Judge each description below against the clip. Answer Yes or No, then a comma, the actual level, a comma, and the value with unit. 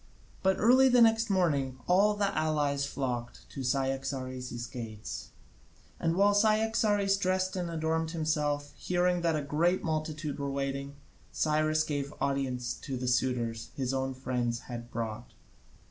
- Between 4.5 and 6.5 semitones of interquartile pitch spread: Yes, wide, 5.5 semitones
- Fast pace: No, average, 140 wpm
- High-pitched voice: No, medium, 145 Hz